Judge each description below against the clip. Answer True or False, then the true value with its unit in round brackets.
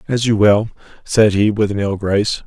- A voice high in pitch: False (105 Hz)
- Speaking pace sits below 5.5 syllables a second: True (5.1 syllables/s)